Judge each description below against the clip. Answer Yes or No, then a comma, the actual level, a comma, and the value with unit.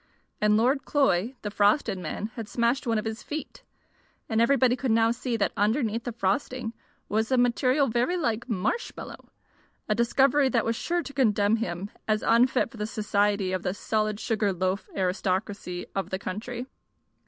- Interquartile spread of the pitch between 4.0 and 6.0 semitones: No, average, 3.4 semitones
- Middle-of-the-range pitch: No, high, 225 Hz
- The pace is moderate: Yes, average, 170 wpm